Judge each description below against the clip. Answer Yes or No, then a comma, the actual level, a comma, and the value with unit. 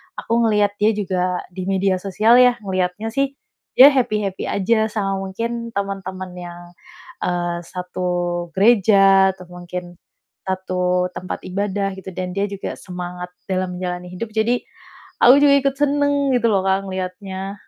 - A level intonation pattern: No, average, 3.2 semitones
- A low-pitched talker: No, high, 190 Hz